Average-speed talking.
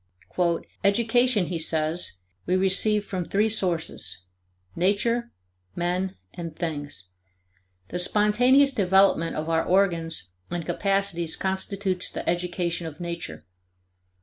No: slow, 105 wpm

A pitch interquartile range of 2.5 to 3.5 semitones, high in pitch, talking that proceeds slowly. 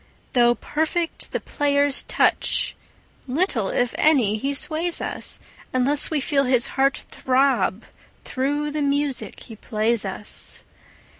Yes: average, 3.2 semitones; very high, 275 Hz; slow, 125 wpm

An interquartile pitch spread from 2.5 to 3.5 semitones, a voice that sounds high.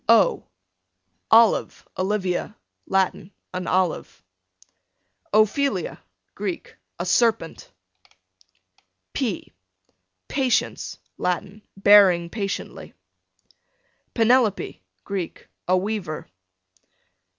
Yes: average, 3.1 semitones; high, 195 Hz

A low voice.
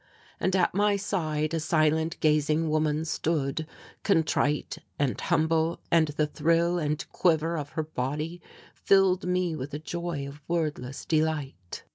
No: medium, 160 Hz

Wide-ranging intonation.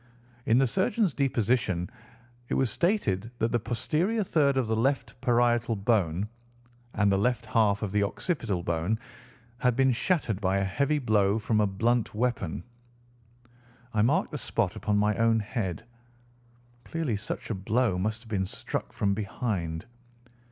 No: average, 4.0 semitones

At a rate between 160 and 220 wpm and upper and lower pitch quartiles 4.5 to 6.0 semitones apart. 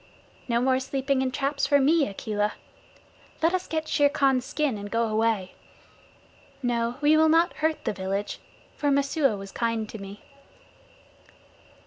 No: average, 150 wpm; average, 5.1 semitones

